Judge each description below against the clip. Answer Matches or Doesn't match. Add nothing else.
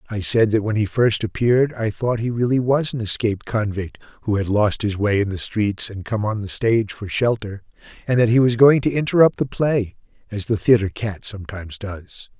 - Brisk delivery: Matches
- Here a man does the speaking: Matches